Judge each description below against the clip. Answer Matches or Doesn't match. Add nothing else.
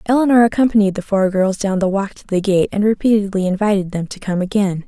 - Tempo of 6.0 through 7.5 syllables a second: Matches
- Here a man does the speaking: Doesn't match